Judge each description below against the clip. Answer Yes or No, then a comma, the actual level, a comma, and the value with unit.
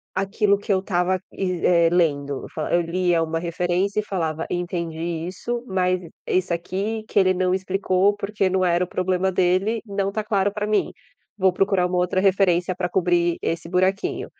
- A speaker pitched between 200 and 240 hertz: No, medium, 185 Hz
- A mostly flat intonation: Yes, narrow, 2.0 semitones